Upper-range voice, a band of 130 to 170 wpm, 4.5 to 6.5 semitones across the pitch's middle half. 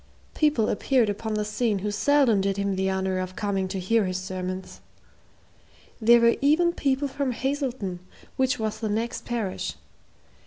Yes: high, 215 Hz; average, 160 wpm; average, 5.1 semitones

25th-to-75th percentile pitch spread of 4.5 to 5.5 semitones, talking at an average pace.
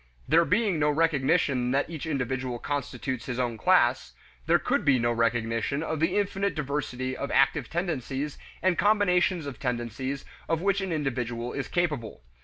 Yes: average, 5.1 semitones; average, 160 wpm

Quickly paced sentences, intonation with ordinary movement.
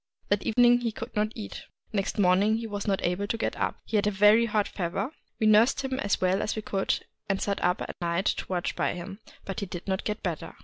No: fast, 255 wpm; narrow, 2.3 semitones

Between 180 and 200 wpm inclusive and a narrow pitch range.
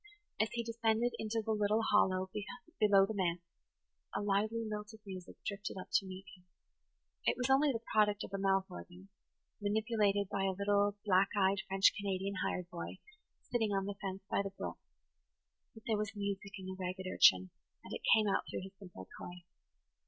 Yes: average, 185 wpm; narrow, 2.1 semitones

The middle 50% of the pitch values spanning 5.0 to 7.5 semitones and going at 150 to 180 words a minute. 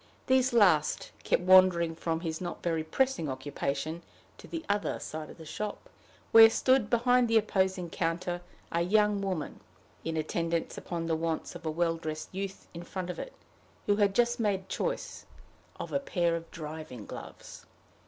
No: average, 4.3 semitones; average, 170 wpm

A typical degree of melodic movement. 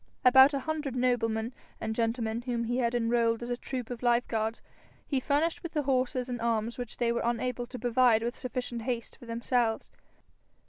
No: narrow, 1.7 semitones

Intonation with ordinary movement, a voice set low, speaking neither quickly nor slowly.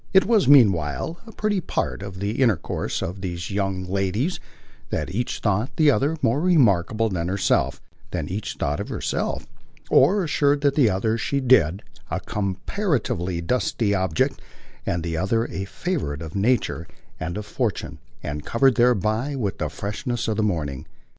No: wide, 6.4 semitones; low, 105 Hz; average, 155 wpm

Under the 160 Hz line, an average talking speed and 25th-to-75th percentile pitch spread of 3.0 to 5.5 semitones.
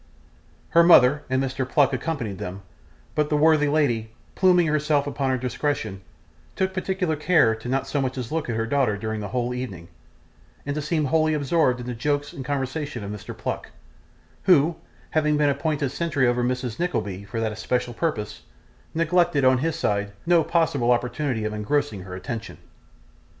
Yes: low, 135 Hz; average, 175 wpm; average, 4.6 semitones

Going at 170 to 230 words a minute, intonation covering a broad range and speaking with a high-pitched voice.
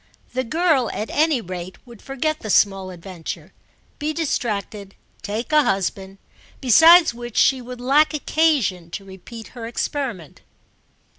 No: slow, 135 wpm; wide, 7.0 semitones; high, 235 Hz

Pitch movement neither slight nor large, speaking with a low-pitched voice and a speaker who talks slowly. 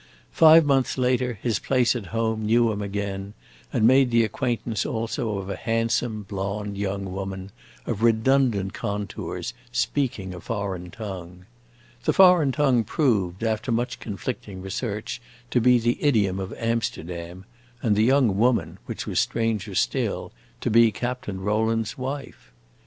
No: average, 3.8 semitones; low, 110 Hz; average, 145 wpm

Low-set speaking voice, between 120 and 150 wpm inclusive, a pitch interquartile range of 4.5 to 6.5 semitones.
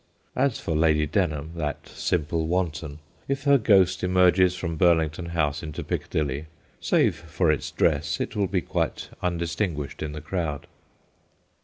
No: very low, 85 Hz; average, 145 wpm; average, 3.1 semitones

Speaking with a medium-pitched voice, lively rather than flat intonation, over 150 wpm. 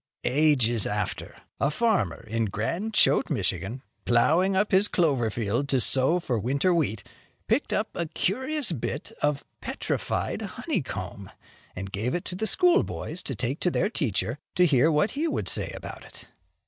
Yes: medium, 145 Hz; wide, 7.5 semitones; average, 160 wpm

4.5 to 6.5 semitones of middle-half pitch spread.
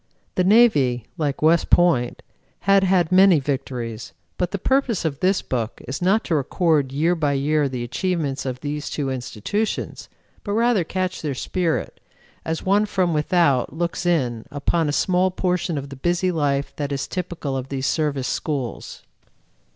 Yes: average, 5.0 semitones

